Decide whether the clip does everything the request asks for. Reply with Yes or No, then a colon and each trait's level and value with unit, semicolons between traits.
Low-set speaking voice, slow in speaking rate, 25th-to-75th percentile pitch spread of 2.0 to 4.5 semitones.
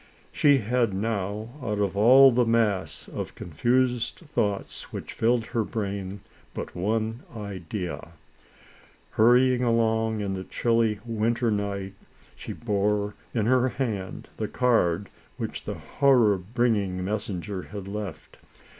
Yes: low, 110 Hz; slow, 125 wpm; average, 3.0 semitones